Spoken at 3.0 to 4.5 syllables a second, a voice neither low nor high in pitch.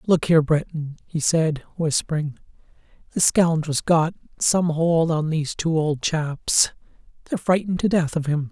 No: 4.7 syllables/s; medium, 160 Hz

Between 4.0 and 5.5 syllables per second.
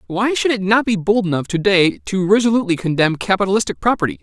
No: 6.4 syllables/s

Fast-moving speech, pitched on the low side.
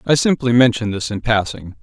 No: average, 195 wpm; low, 115 Hz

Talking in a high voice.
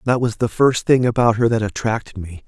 No: low, 115 Hz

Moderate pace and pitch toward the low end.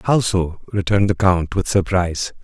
Yes: average, 175 wpm; very low, 95 Hz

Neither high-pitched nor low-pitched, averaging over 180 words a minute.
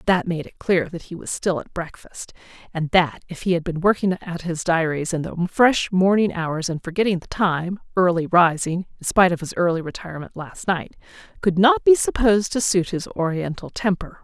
Yes: medium, 180 Hz; average, 200 wpm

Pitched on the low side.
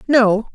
No: high, 230 Hz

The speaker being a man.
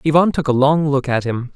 Yes: male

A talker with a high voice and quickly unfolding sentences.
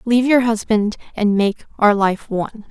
No: high, 215 Hz; average, 180 wpm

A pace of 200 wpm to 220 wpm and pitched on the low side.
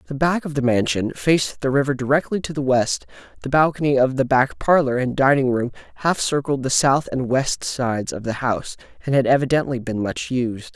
Yes: fast, 205 wpm; low, 130 Hz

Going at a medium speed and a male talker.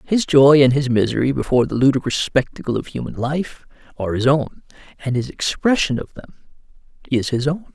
Yes: average, 180 wpm; male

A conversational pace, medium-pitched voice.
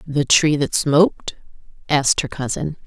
Yes: average, 145 wpm; medium, 145 Hz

